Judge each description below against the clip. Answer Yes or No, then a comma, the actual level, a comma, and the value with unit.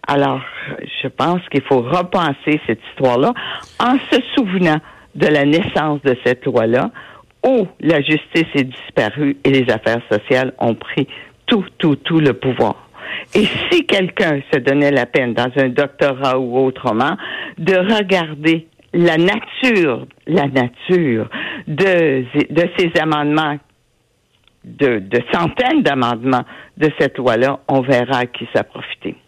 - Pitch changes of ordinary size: Yes, average, 4.6 semitones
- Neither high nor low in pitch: Yes, medium, 145 Hz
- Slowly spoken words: Yes, slow, 135 wpm